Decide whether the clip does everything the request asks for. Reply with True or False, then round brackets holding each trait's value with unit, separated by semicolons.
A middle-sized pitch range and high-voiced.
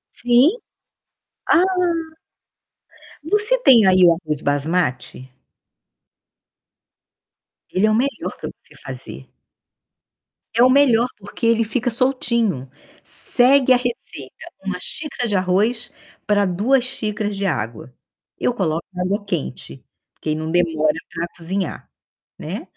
False (6.6 semitones; 205 Hz)